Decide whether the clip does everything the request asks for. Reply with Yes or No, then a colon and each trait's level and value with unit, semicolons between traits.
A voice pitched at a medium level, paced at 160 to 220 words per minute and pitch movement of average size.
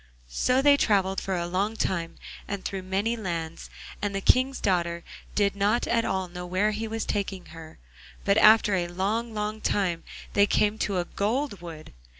No: high, 200 Hz; average, 180 wpm; average, 3.3 semitones